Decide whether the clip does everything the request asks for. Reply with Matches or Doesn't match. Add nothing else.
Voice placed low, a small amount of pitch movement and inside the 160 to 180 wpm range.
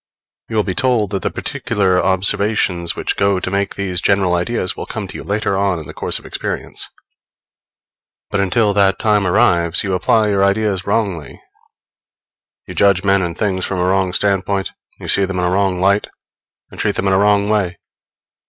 Doesn't match